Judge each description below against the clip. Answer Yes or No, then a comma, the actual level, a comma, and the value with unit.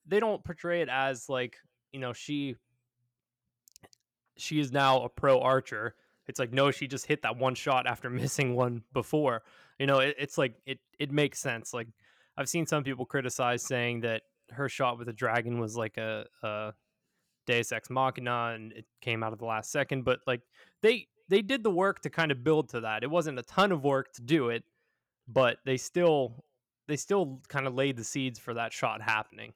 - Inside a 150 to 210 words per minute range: Yes, fast, 205 wpm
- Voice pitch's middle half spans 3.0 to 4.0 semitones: Yes, average, 3.4 semitones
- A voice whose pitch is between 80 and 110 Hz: No, low, 130 Hz